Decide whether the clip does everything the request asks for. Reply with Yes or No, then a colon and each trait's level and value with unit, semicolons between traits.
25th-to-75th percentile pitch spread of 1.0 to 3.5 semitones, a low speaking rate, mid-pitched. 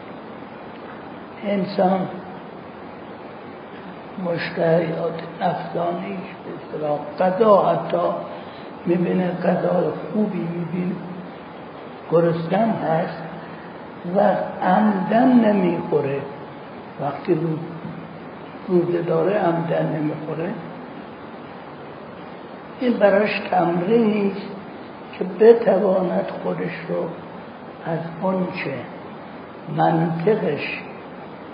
Yes: average, 3.2 semitones; slow, 55 wpm; medium, 180 Hz